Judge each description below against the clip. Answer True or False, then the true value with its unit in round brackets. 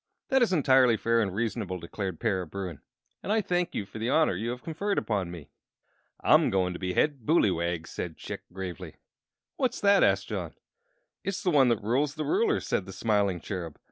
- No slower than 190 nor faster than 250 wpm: True (195 wpm)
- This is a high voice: False (110 Hz)